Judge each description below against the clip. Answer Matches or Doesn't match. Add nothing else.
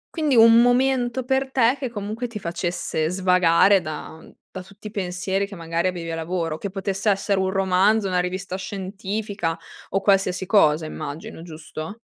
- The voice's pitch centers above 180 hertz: Matches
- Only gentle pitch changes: Doesn't match